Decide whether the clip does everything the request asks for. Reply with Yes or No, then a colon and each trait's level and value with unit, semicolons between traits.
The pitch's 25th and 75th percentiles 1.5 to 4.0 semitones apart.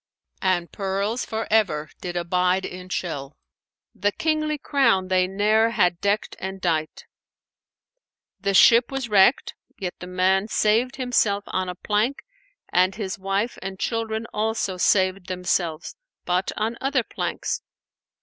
Yes: average, 3.3 semitones